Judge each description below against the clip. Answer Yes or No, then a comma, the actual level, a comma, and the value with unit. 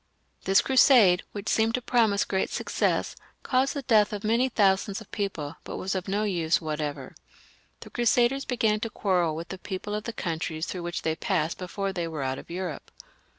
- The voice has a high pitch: Yes, high, 195 Hz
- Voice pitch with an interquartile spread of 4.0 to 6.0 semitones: Yes, average, 4.6 semitones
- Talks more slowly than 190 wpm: No, average, 195 wpm